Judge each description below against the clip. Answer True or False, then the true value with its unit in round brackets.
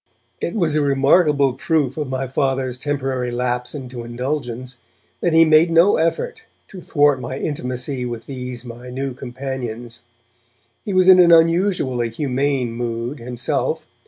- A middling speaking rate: True (145 wpm)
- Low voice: True (130 Hz)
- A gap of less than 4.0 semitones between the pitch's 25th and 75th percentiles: True (3.6 semitones)